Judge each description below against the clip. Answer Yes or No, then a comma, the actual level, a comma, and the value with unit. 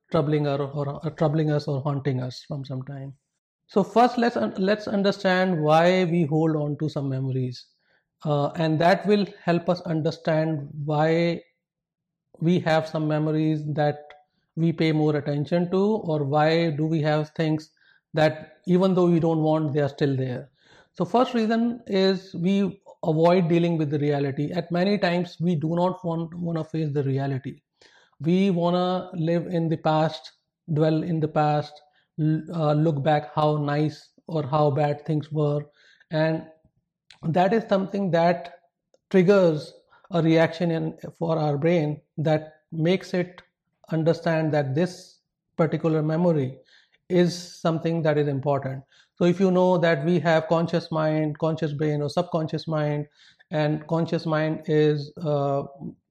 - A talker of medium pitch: Yes, medium, 160 Hz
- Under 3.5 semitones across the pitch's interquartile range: Yes, narrow, 2.5 semitones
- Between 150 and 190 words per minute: Yes, average, 155 wpm